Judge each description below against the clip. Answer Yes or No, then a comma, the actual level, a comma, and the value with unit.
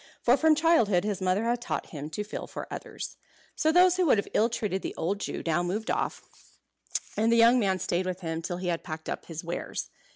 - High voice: Yes, high, 200 Hz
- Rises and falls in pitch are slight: No, average, 5.0 semitones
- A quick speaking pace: Yes, fast, 230 wpm